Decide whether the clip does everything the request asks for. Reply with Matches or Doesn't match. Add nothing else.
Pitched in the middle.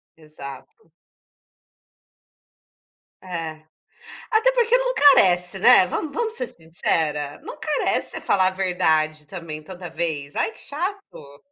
Matches